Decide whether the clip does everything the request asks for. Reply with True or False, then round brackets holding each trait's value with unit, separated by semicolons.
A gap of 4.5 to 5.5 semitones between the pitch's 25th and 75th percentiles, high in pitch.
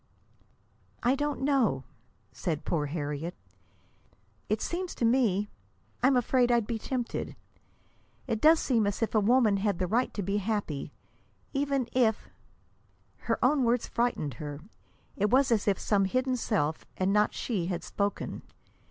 True (4.9 semitones; 220 Hz)